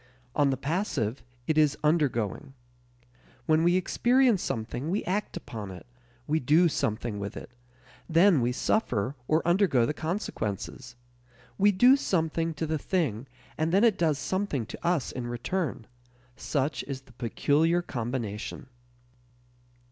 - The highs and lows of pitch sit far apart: Yes, wide, 6.2 semitones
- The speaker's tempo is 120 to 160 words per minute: Yes, average, 140 wpm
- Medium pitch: Yes, medium, 150 Hz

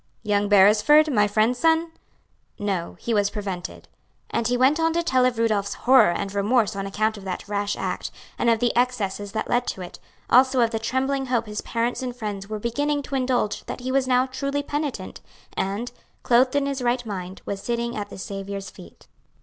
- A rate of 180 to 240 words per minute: Yes, average, 200 wpm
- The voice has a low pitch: No, high, 230 Hz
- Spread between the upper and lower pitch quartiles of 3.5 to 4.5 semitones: Yes, average, 4.2 semitones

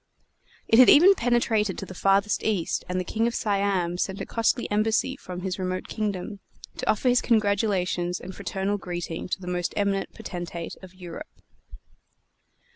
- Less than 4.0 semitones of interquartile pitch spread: Yes, average, 3.2 semitones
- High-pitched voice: Yes, high, 195 Hz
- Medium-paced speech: Yes, average, 165 wpm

